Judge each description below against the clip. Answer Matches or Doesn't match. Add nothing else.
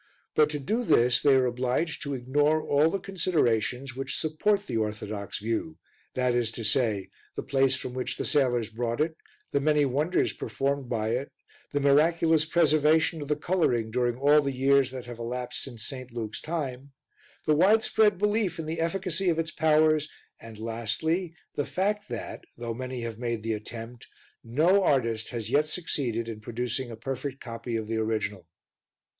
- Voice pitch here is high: Doesn't match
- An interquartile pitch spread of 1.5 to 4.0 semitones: Doesn't match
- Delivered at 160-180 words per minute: Matches